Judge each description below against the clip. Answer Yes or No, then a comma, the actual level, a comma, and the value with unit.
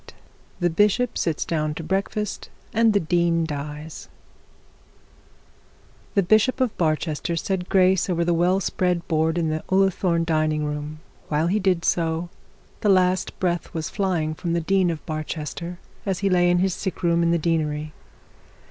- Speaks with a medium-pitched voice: Yes, medium, 170 Hz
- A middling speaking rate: Yes, average, 170 wpm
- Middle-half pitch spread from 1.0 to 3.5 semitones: Yes, average, 3.0 semitones